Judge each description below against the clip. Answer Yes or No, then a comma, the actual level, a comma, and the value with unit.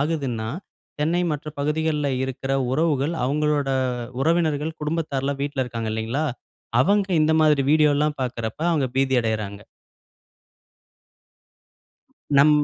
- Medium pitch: Yes, medium, 145 Hz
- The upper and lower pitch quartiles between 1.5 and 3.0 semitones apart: Yes, average, 2.7 semitones